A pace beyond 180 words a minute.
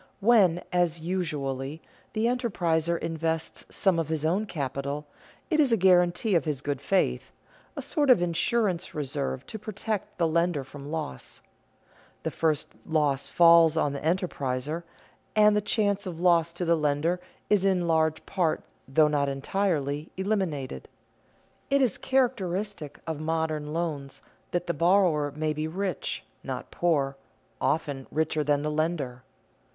No: average, 145 wpm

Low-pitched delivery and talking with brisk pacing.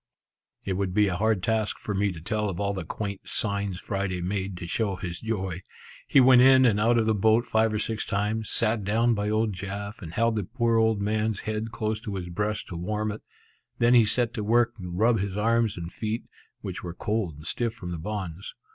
Yes: low, 105 Hz; fast, 225 wpm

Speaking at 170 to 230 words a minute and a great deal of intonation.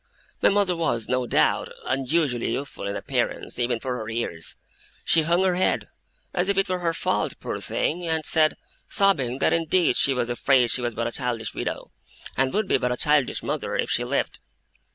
Yes: average, 195 wpm; wide, 5.8 semitones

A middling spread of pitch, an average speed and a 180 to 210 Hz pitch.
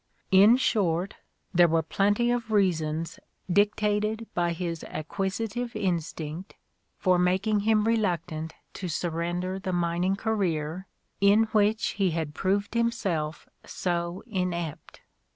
No: average, 3.7 semitones; slow, 115 wpm; medium, 185 Hz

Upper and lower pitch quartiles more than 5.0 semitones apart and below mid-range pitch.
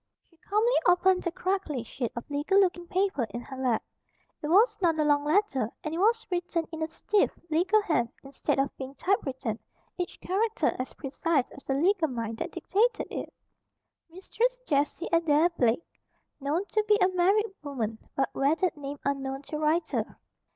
No: wide, 5.6 semitones; very high, 320 Hz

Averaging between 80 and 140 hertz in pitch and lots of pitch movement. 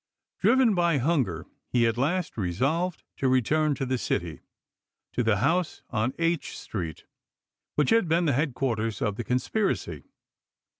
Yes: low, 135 Hz; wide, 6.6 semitones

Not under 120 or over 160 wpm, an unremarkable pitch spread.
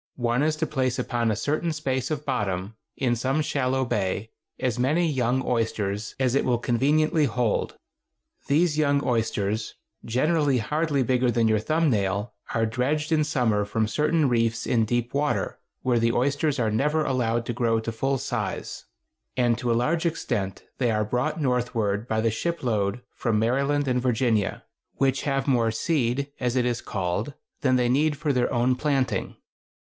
No: average, 175 wpm; average, 3.9 semitones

